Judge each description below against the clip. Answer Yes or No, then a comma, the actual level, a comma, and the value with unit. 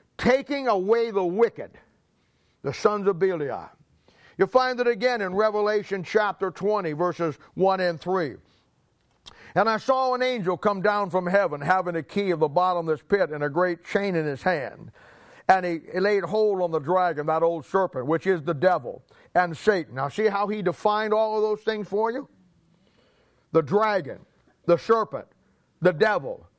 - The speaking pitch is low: No, high, 195 Hz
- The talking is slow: No, average, 175 wpm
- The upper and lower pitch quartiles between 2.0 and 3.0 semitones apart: No, average, 3.5 semitones